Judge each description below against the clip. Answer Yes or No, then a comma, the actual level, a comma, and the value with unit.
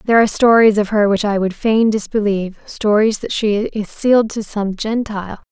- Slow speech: No, average, 185 wpm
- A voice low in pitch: No, high, 210 Hz